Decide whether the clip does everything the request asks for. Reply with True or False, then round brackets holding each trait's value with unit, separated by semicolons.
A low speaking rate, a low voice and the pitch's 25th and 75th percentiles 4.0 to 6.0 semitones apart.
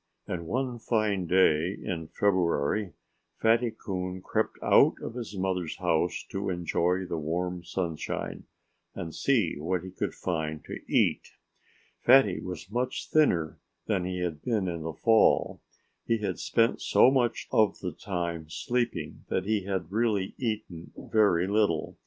False (145 wpm; 95 Hz; 4.3 semitones)